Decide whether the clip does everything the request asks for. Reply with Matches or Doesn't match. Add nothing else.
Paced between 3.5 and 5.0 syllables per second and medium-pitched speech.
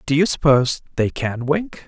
Matches